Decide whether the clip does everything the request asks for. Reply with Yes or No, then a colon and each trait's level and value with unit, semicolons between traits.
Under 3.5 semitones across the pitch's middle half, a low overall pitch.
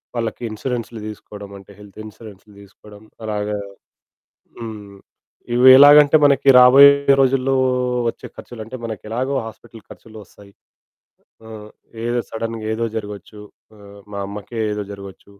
Yes: average, 2.8 semitones; low, 110 Hz